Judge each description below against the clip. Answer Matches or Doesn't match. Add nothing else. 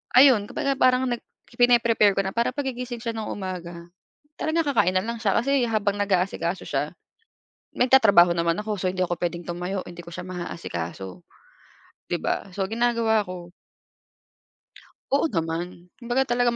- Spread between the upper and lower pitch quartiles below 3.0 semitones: Doesn't match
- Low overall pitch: Doesn't match